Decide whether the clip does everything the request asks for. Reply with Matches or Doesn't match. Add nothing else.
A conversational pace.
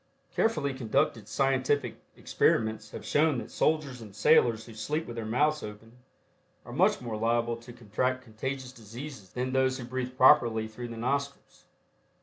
Matches